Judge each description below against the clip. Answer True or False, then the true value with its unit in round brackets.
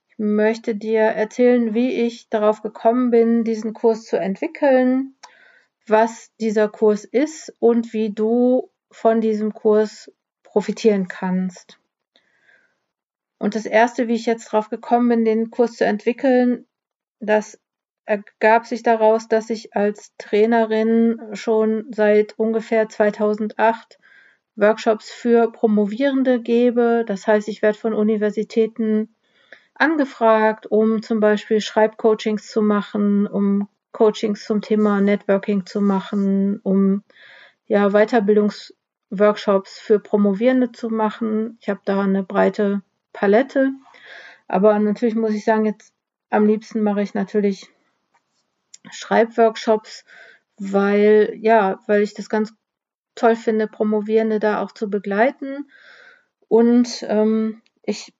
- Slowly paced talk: True (120 wpm)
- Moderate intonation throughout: False (1.7 semitones)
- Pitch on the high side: True (220 Hz)